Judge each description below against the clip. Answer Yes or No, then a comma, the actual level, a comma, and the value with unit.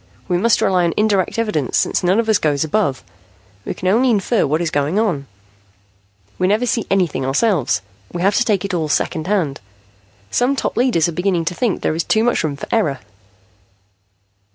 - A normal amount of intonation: No, wide, 5.7 semitones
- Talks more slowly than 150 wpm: No, average, 185 wpm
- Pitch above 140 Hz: Yes, medium, 185 Hz